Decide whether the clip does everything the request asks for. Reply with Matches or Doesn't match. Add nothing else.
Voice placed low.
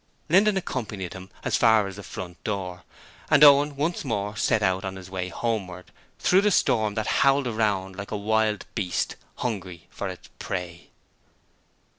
Matches